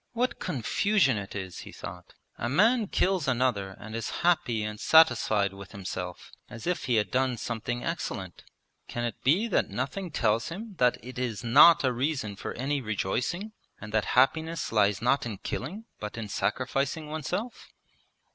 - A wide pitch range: Yes, wide, 7.0 semitones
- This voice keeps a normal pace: Yes, average, 165 wpm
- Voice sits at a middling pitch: No, low, 125 Hz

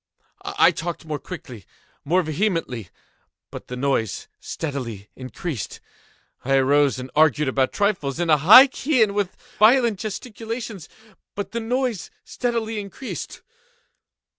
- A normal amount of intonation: No, wide, 8.2 semitones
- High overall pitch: No, medium, 175 Hz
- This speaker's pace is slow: Yes, slow, 120 wpm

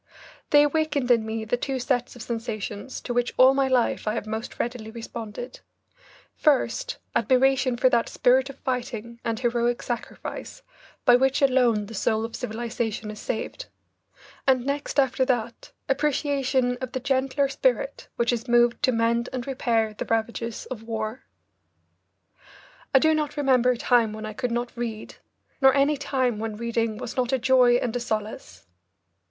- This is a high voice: Yes, high, 245 Hz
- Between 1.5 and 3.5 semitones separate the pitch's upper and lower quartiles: Yes, narrow, 2.6 semitones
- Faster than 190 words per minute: No, average, 165 wpm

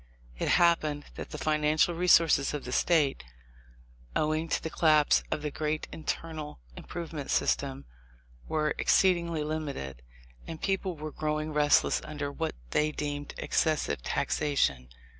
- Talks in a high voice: No, medium, 155 Hz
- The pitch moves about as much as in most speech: No, narrow, 1.7 semitones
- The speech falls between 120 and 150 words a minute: Yes, slow, 135 wpm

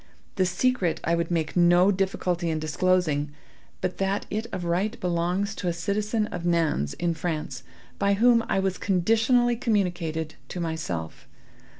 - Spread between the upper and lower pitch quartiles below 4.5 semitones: Yes, average, 3.1 semitones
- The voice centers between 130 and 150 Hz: No, medium, 180 Hz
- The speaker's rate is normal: Yes, average, 155 wpm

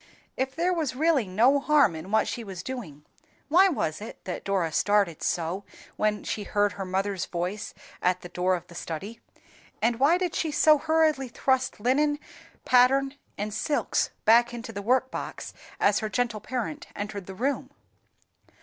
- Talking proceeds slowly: No, average, 165 wpm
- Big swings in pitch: Yes, wide, 5.9 semitones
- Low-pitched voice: No, high, 225 Hz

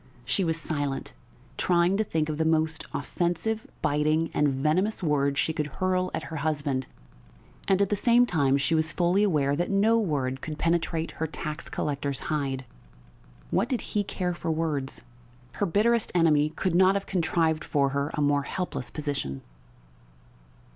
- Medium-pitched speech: Yes, medium, 160 Hz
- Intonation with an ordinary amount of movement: Yes, average, 4.1 semitones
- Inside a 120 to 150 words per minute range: No, average, 165 wpm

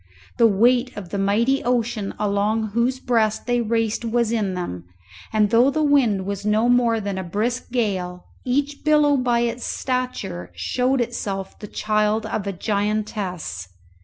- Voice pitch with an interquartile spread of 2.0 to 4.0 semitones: Yes, average, 3.4 semitones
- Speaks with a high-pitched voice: Yes, high, 220 Hz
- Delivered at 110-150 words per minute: No, average, 160 wpm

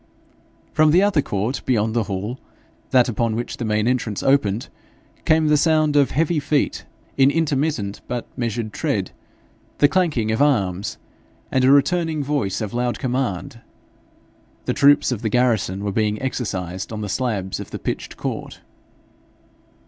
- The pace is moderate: Yes, average, 155 wpm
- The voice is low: Yes, low, 125 Hz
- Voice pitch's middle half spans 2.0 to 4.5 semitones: No, average, 5.2 semitones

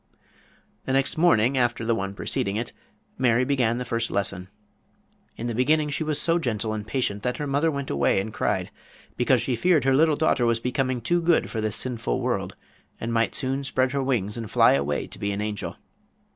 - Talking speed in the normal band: No, fast, 210 wpm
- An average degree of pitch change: Yes, average, 3.8 semitones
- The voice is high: No, low, 125 Hz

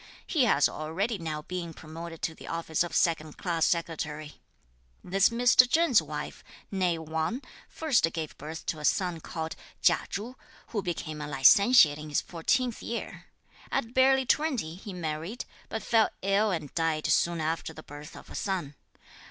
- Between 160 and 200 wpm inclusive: Yes, average, 165 wpm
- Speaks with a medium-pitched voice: Yes, medium, 170 Hz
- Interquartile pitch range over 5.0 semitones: Yes, wide, 5.6 semitones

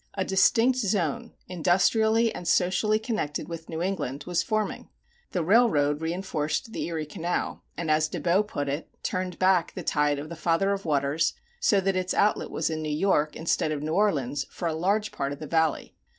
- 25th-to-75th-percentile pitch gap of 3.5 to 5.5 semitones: Yes, average, 4.2 semitones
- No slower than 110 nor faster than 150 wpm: No, average, 195 wpm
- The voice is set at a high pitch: No, medium, 170 Hz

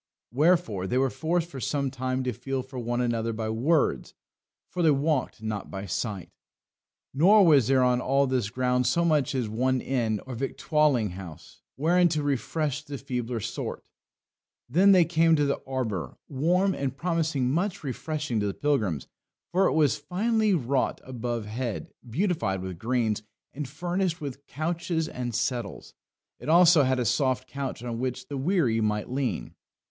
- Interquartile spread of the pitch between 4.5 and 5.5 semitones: Yes, average, 4.8 semitones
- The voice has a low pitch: Yes, low, 130 Hz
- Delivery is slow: No, average, 165 wpm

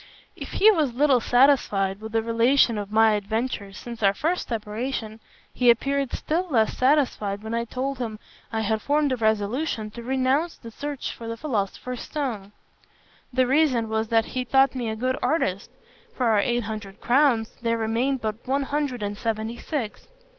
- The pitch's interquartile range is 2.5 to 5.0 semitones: Yes, average, 3.5 semitones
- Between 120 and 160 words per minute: No, average, 175 wpm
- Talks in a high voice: Yes, high, 235 Hz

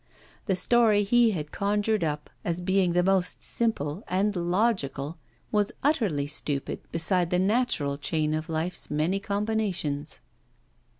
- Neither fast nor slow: No, slow, 130 wpm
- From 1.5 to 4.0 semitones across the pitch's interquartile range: No, average, 5.1 semitones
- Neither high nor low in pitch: Yes, medium, 180 Hz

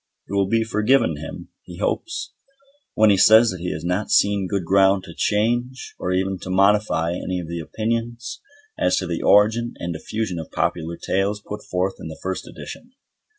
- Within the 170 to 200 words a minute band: Yes, average, 190 wpm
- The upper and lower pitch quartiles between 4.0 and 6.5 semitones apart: No, average, 3.5 semitones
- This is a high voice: No, low, 100 Hz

